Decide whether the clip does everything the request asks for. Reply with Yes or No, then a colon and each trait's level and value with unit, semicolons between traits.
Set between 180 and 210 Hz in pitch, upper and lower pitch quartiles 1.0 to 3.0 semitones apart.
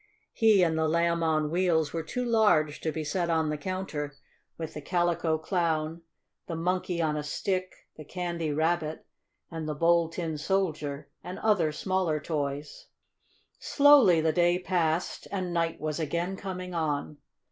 No: medium, 165 Hz; average, 2.7 semitones